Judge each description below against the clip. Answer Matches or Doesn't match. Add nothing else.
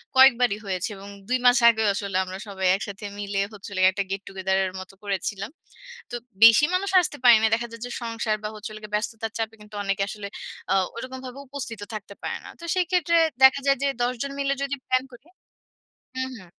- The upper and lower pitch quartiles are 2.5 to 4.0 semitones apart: Doesn't match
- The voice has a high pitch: Matches